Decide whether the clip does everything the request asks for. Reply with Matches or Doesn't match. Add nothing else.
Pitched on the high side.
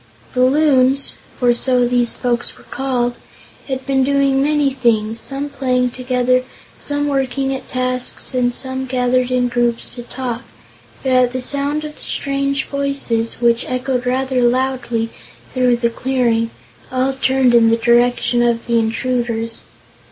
Matches